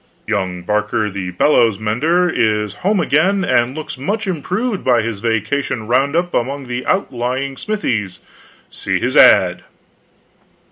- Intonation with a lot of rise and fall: Yes, wide, 7.8 semitones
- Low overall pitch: Yes, low, 125 Hz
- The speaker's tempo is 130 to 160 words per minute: Yes, average, 140 wpm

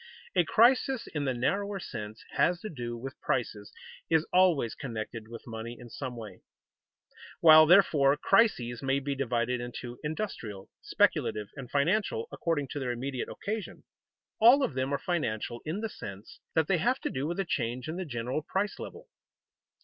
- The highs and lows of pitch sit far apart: Yes, wide, 7.0 semitones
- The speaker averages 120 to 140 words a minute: No, average, 170 wpm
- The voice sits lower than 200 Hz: Yes, medium, 140 Hz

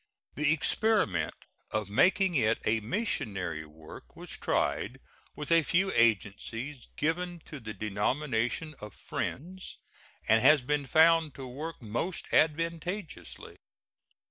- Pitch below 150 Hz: Yes, medium, 140 Hz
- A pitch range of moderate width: No, wide, 7.3 semitones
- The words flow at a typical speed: No, slow, 115 wpm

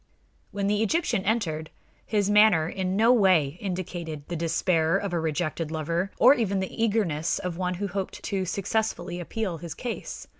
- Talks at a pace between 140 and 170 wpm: Yes, average, 165 wpm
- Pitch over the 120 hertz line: Yes, medium, 185 Hz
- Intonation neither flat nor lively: Yes, average, 3.7 semitones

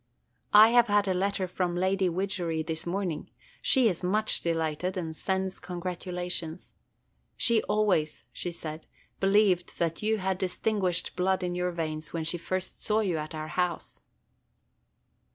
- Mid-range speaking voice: Yes, medium, 180 Hz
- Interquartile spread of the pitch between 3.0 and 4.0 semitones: No, narrow, 2.6 semitones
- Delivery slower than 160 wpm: Yes, average, 150 wpm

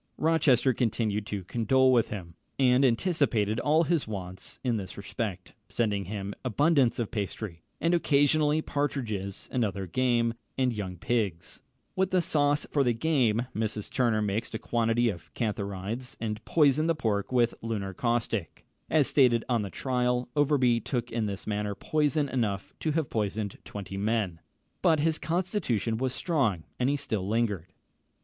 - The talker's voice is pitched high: No, low, 115 Hz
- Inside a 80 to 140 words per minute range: No, average, 155 wpm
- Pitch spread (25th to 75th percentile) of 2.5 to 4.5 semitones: No, average, 5.1 semitones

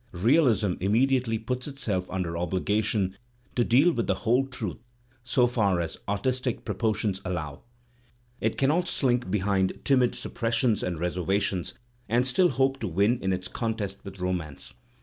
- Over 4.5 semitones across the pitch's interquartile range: Yes, average, 5.1 semitones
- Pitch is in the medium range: No, low, 110 Hz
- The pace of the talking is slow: No, average, 145 wpm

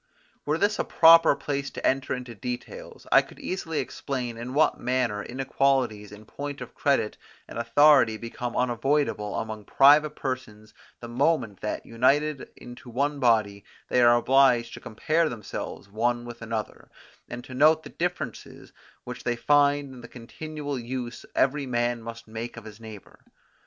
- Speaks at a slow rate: No, average, 160 wpm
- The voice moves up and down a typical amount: Yes, average, 3.6 semitones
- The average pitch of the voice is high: No, low, 125 Hz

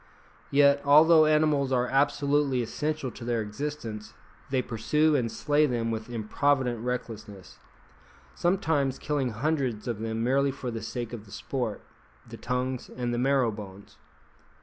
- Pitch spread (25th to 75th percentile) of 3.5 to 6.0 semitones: Yes, average, 4.0 semitones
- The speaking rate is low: No, average, 145 wpm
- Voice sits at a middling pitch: No, low, 125 Hz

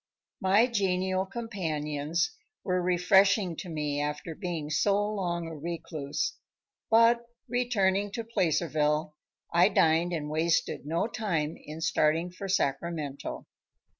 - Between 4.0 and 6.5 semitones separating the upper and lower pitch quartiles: Yes, average, 4.3 semitones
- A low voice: No, medium, 175 Hz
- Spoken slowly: Yes, slow, 115 wpm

